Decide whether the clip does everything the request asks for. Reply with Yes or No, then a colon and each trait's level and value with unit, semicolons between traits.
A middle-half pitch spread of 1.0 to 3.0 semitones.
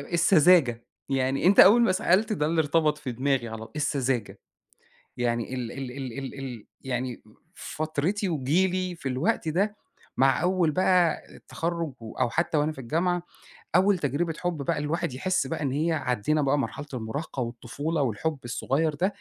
No: average, 4.7 semitones